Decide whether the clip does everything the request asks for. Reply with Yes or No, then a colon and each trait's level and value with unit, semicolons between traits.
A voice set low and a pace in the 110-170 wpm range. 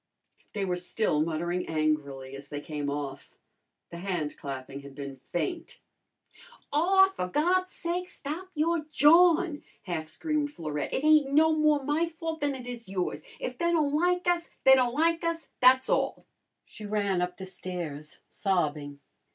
No: high, 240 Hz; average, 160 wpm